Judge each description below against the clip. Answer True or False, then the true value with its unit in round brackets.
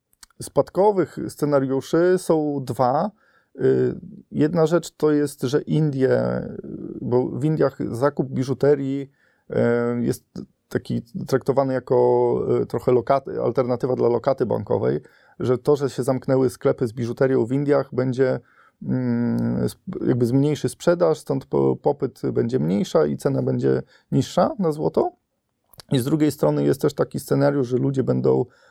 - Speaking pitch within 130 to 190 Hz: True (135 Hz)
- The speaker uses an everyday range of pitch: True (3.6 semitones)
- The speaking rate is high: False (125 wpm)